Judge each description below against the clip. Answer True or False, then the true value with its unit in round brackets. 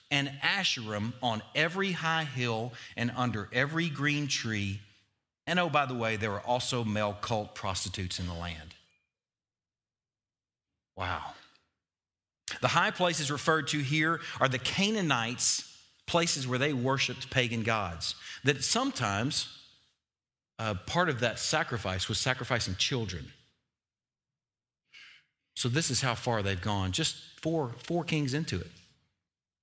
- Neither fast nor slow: False (130 wpm)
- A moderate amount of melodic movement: False (5.9 semitones)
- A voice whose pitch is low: True (125 Hz)